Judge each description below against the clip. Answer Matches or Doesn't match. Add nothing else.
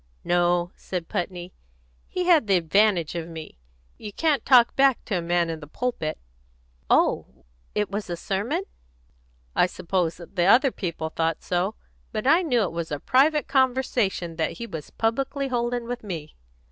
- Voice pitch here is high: Matches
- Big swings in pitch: Matches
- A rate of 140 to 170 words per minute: Matches